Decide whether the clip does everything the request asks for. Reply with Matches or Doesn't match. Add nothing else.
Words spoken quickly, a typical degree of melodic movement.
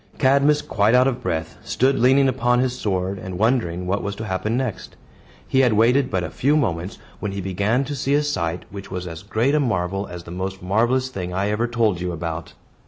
Doesn't match